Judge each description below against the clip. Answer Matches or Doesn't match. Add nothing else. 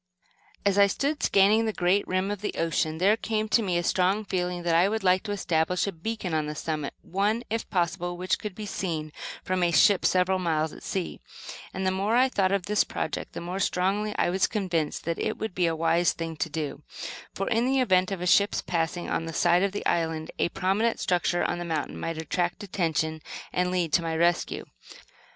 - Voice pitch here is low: Doesn't match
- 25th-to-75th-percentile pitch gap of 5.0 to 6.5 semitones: Doesn't match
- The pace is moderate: Doesn't match